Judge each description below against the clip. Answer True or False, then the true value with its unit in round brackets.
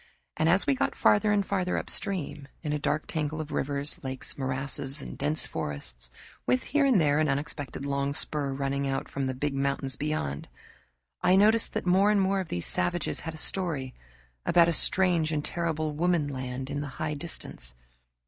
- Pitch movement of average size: True (4.0 semitones)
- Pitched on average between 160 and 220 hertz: False (150 Hz)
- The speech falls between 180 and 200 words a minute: True (185 wpm)